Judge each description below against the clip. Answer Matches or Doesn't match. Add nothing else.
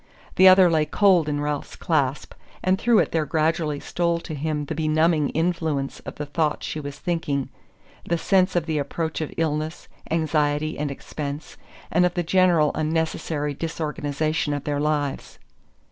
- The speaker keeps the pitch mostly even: Matches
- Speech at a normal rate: Matches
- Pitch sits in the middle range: Matches